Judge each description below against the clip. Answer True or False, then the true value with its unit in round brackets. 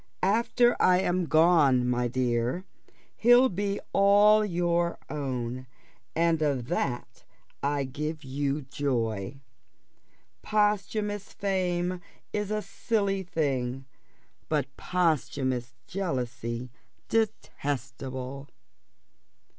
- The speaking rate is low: True (85 wpm)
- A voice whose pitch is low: False (155 Hz)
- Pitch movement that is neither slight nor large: False (7.0 semitones)